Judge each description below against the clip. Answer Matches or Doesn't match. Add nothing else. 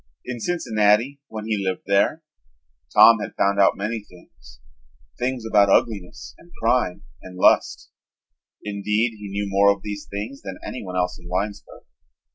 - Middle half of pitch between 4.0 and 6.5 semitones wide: Doesn't match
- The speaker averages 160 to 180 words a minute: Doesn't match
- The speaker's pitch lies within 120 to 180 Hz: Doesn't match